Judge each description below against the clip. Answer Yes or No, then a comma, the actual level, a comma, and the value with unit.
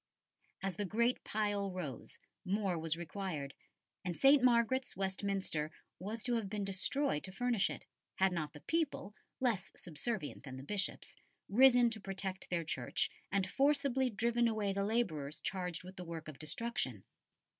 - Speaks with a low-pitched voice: No, high, 195 Hz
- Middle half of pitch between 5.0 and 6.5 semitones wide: Yes, average, 5.3 semitones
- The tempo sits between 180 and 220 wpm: No, average, 155 wpm